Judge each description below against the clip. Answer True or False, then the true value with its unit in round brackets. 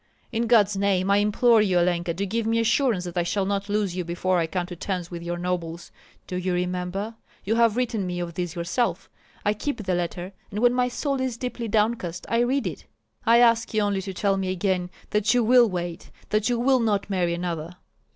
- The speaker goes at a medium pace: False (220 wpm)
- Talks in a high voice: True (195 Hz)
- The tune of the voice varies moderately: True (4.3 semitones)